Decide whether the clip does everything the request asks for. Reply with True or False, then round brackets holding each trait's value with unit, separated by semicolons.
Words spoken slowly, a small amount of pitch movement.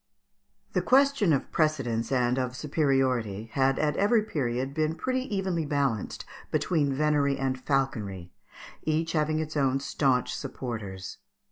False (130 wpm; 3.7 semitones)